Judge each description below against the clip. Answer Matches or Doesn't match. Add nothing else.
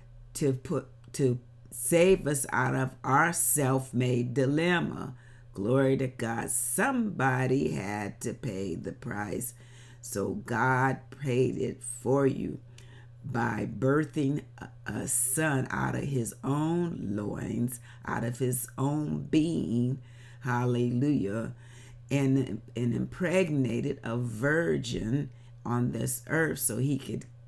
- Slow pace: Matches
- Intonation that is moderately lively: Doesn't match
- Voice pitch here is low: Matches